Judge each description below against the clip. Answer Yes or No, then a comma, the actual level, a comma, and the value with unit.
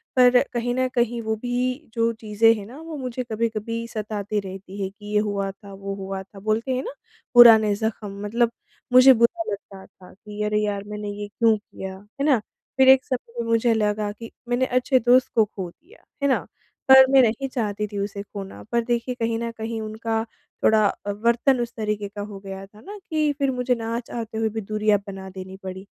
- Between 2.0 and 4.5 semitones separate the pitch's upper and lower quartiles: Yes, average, 2.9 semitones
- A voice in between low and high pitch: No, high, 220 Hz